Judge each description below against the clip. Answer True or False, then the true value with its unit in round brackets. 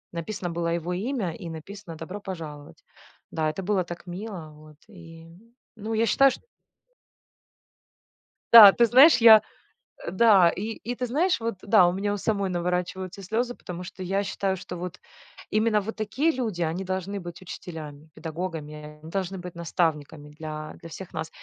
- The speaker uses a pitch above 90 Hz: True (185 Hz)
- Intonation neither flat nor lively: True (4.2 semitones)